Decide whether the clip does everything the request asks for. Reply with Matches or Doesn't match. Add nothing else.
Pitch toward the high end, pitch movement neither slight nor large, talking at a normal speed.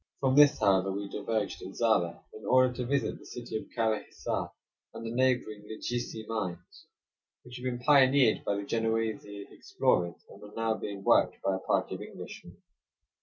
Doesn't match